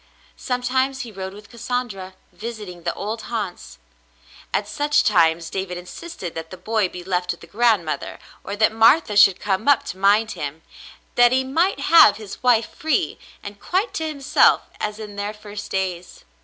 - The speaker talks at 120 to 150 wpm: No, average, 170 wpm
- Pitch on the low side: No, high, 210 Hz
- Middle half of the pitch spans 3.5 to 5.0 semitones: Yes, average, 4.5 semitones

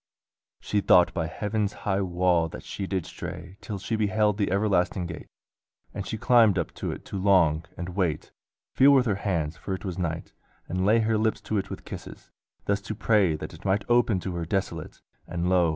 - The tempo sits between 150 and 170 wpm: No, fast, 205 wpm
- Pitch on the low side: Yes, very low, 95 Hz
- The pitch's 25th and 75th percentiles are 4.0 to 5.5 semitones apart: No, average, 3.1 semitones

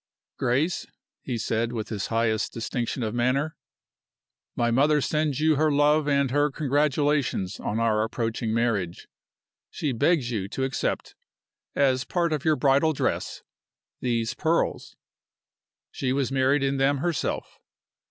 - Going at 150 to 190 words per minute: No, slow, 135 wpm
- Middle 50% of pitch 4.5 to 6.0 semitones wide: No, average, 4.1 semitones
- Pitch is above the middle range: No, low, 135 Hz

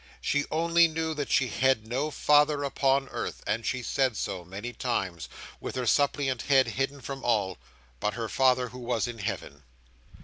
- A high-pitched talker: No, low, 130 Hz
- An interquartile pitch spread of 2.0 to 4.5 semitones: Yes, average, 3.8 semitones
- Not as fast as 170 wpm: No, average, 175 wpm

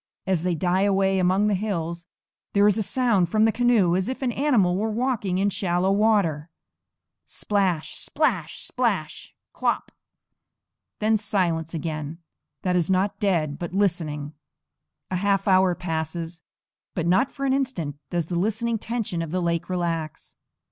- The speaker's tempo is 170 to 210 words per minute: No, average, 155 wpm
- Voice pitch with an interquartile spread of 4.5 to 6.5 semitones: No, average, 3.8 semitones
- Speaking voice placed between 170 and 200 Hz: Yes, medium, 185 Hz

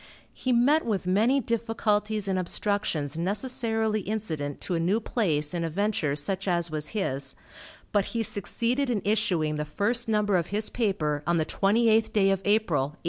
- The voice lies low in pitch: No, high, 200 Hz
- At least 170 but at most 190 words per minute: Yes, average, 180 wpm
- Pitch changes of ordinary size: Yes, average, 4.9 semitones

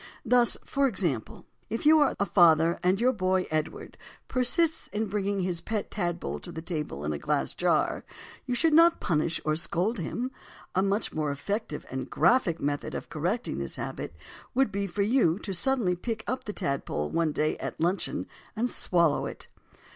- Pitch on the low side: No, high, 190 Hz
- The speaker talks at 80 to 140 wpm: No, average, 180 wpm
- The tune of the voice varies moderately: No, wide, 6.2 semitones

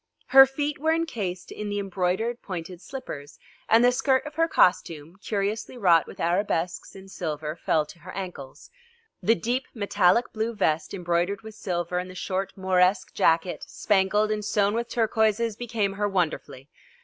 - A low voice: No, high, 195 Hz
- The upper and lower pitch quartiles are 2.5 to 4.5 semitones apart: Yes, average, 4.1 semitones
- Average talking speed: Yes, average, 160 wpm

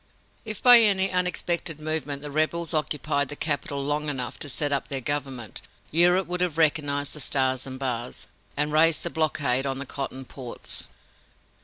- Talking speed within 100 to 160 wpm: No, average, 170 wpm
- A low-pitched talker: No, medium, 145 Hz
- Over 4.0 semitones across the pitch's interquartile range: No, average, 3.1 semitones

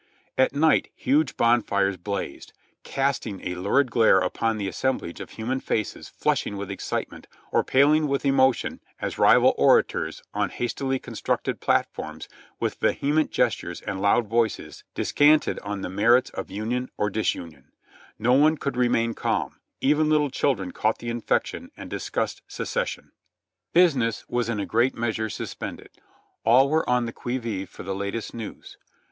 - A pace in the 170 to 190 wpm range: No, average, 155 wpm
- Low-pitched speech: Yes, low, 120 Hz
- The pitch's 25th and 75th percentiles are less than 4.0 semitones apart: No, average, 4.8 semitones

